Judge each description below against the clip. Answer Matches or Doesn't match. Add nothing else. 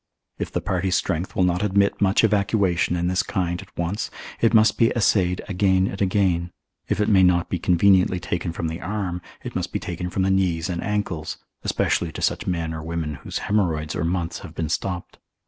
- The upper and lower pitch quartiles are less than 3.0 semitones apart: Matches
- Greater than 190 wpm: Matches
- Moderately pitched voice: Doesn't match